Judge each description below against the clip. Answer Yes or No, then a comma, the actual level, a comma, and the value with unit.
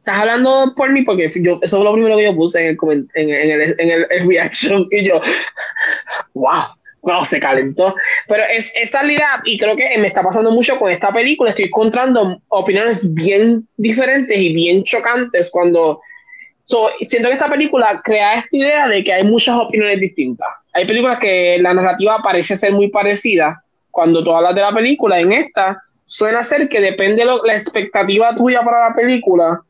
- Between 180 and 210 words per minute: Yes, fast, 190 wpm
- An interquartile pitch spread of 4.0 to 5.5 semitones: Yes, average, 4.7 semitones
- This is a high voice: Yes, high, 215 Hz